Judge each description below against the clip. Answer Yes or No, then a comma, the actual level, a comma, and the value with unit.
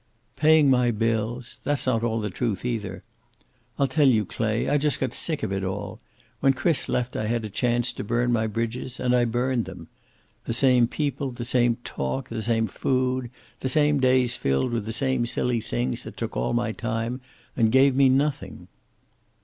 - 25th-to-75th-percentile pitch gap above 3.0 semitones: No, average, 2.7 semitones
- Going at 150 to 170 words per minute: No, average, 190 wpm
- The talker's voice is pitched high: No, low, 120 Hz